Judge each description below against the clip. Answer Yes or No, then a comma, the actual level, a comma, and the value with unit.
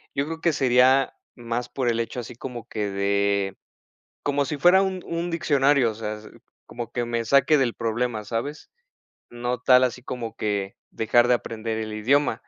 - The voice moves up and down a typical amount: Yes, average, 3.7 semitones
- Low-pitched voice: Yes, low, 120 Hz